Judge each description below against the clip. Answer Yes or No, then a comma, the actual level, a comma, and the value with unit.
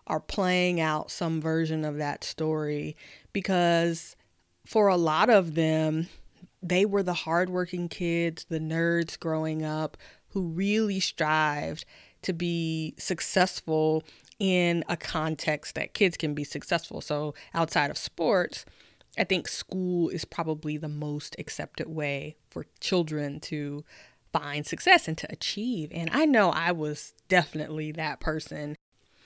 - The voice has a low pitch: No, medium, 160 Hz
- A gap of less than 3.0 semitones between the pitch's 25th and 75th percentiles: Yes, narrow, 2.6 semitones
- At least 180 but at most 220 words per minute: No, slow, 135 wpm